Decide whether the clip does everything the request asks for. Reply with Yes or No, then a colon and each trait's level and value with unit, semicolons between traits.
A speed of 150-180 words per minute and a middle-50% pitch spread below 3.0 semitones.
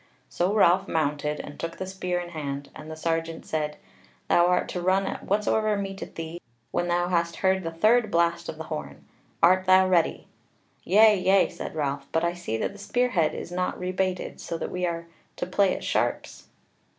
No: average, 200 wpm; narrow, 2.5 semitones